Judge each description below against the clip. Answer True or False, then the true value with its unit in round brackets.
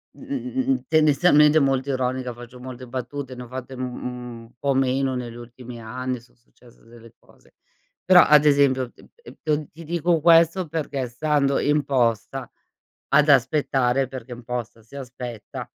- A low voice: True (130 Hz)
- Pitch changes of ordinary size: True (3.3 semitones)